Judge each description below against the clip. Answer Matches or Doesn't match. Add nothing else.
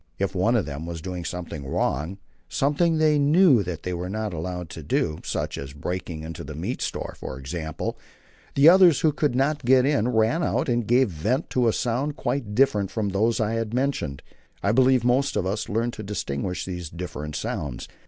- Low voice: Matches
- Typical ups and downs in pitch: Doesn't match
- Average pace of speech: Matches